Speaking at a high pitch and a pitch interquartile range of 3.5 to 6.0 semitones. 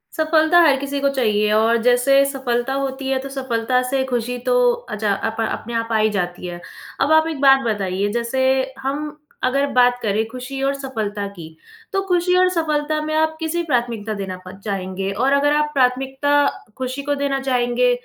Yes: very high, 260 Hz; average, 4.0 semitones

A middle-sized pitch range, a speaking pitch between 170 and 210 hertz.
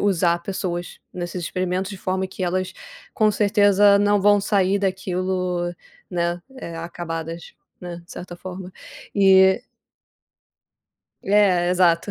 No: narrow, 2.0 semitones; medium, 185 Hz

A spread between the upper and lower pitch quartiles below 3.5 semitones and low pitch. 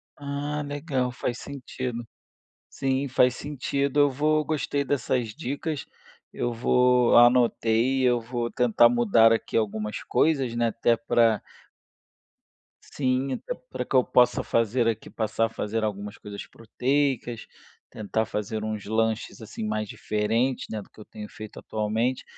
Yes: average, 3.1 semitones; low, 120 Hz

